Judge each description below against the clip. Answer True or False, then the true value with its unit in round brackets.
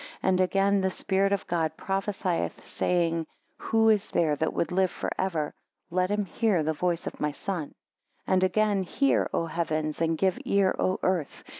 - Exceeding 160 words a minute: True (180 wpm)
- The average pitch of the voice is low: False (185 Hz)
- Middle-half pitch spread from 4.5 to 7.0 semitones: False (2.9 semitones)